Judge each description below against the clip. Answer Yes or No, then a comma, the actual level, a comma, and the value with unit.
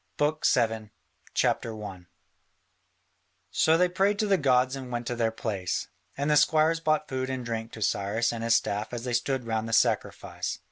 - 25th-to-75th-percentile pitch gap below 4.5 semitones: No, average, 4.8 semitones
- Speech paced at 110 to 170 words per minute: No, average, 180 wpm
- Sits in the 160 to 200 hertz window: No, low, 120 Hz